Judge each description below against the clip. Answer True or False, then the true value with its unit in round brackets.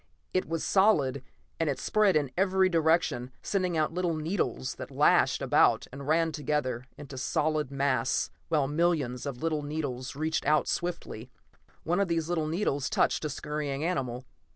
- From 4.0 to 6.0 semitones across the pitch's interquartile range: False (3.6 semitones)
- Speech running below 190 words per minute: True (165 wpm)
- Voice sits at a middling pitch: True (155 Hz)